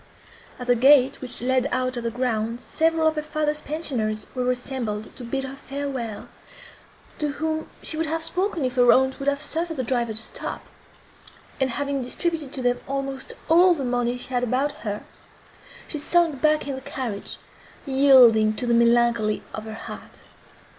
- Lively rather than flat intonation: No, average, 3.6 semitones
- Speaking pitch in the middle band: No, very high, 260 Hz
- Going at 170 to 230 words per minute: Yes, average, 180 wpm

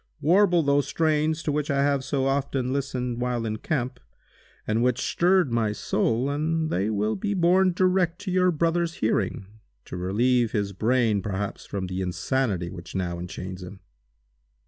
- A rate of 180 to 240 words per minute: No, average, 165 wpm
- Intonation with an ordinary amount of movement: No, wide, 7.2 semitones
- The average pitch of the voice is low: Yes, low, 130 Hz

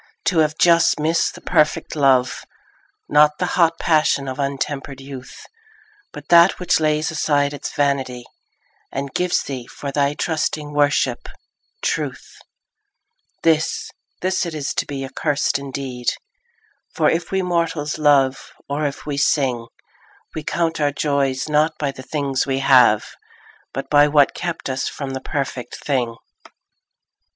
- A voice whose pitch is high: No, medium, 145 Hz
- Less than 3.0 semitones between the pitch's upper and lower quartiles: Yes, narrow, 2.4 semitones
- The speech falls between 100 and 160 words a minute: Yes, average, 145 wpm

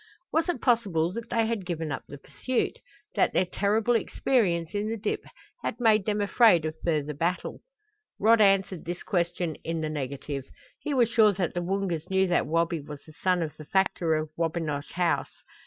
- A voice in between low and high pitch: Yes, medium, 180 Hz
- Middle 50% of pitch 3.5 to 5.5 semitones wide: Yes, average, 4.9 semitones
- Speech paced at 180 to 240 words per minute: Yes, average, 190 wpm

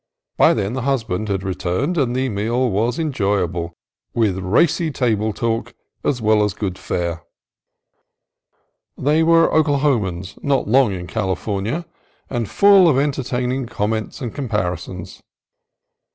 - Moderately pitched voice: No, low, 115 Hz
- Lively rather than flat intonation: Yes, wide, 5.7 semitones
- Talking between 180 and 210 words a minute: No, average, 140 wpm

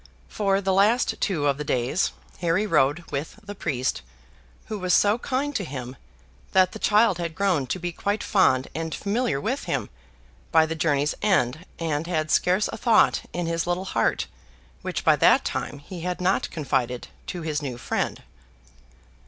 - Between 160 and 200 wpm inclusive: Yes, average, 175 wpm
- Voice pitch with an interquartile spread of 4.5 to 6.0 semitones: Yes, average, 5.2 semitones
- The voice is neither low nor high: Yes, medium, 175 Hz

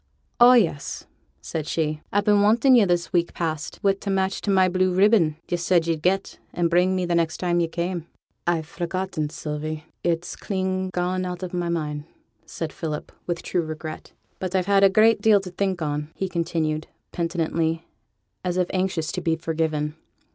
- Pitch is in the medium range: Yes, medium, 175 Hz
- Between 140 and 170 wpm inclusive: No, average, 185 wpm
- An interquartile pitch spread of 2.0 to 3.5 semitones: Yes, average, 2.7 semitones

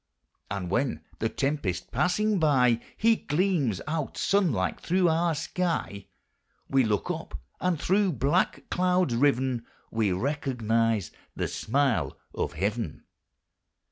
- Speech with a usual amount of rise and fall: No, wide, 7.6 semitones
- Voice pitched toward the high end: No, low, 135 Hz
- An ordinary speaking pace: No, slow, 115 wpm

